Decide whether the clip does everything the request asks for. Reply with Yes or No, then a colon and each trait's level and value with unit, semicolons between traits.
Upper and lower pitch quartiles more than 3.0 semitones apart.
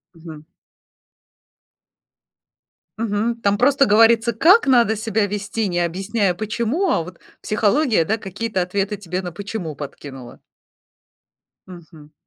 Yes: average, 4.4 semitones